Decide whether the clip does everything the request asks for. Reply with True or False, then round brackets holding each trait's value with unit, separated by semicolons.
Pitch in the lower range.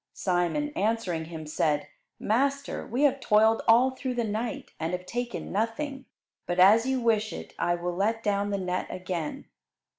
False (215 Hz)